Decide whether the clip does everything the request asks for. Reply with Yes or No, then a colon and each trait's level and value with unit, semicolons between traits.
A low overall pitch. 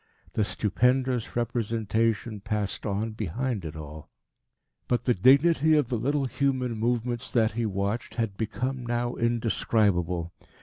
Yes: low, 115 Hz